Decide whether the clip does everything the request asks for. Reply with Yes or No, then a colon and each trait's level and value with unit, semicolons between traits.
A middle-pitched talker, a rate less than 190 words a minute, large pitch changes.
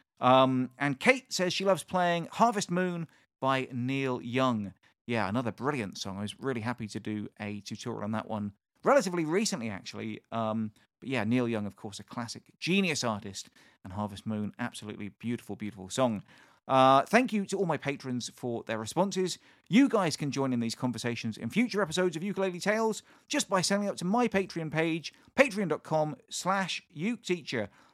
No: low, 130 Hz; average, 175 wpm; wide, 8.6 semitones